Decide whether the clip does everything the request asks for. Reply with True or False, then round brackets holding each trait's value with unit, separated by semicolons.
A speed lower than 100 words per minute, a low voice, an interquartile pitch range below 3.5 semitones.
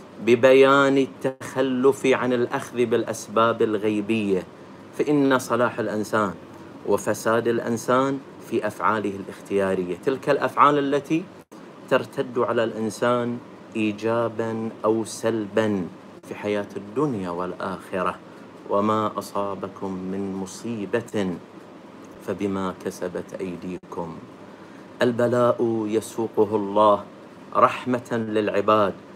True (80 wpm; 115 Hz; 2.9 semitones)